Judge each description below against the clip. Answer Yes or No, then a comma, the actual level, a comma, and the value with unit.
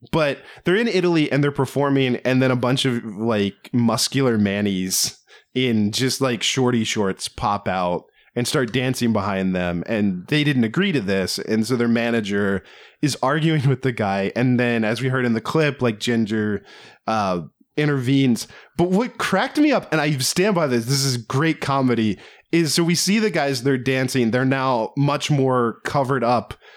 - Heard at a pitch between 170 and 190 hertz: No, low, 125 Hz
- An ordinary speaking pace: Yes, average, 185 wpm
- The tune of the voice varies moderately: Yes, average, 4.0 semitones